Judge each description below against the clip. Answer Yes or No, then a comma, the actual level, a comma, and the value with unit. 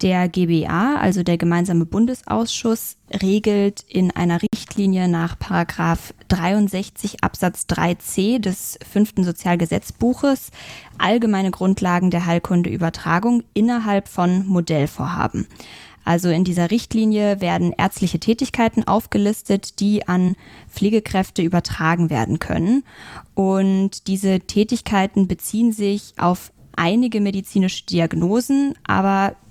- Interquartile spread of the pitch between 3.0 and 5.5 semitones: Yes, average, 3.4 semitones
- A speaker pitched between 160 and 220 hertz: Yes, high, 190 Hz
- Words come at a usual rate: No, slow, 100 wpm